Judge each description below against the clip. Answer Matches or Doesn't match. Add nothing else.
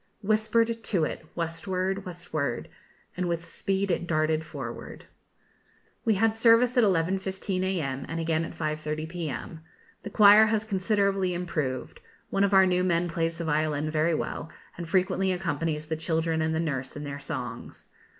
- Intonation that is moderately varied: Matches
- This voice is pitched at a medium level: Matches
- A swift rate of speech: Doesn't match